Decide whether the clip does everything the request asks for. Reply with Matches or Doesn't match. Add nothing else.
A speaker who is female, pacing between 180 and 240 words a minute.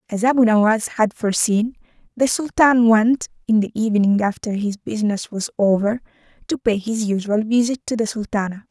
Doesn't match